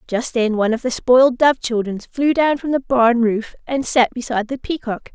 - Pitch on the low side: No, high, 245 Hz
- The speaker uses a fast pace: Yes, fast, 220 wpm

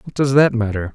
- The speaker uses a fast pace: Yes, fast, 255 wpm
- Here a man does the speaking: Yes, male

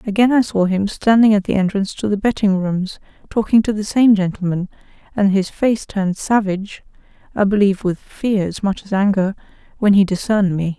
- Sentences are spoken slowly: No, average, 180 wpm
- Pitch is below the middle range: No, high, 200 Hz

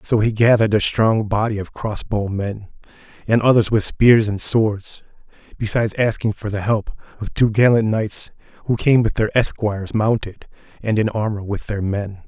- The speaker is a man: Yes, male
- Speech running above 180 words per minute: No, average, 175 wpm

